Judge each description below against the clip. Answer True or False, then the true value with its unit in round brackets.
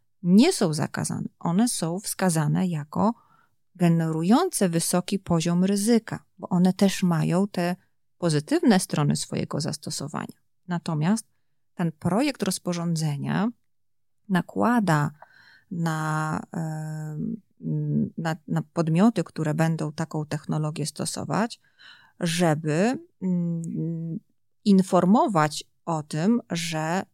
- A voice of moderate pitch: True (175 Hz)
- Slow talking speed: True (85 wpm)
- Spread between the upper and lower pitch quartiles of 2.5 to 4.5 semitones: True (3.9 semitones)